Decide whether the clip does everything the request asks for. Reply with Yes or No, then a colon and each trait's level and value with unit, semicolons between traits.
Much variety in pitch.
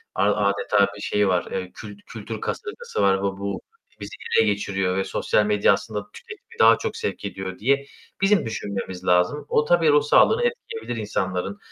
Yes: wide, 7.4 semitones